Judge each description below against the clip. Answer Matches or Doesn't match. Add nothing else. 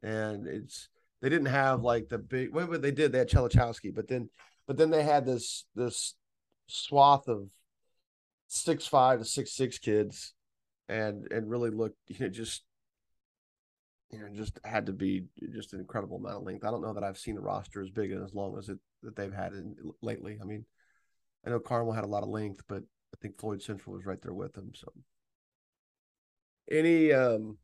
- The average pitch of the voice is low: Matches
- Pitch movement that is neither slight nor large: Matches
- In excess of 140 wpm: Matches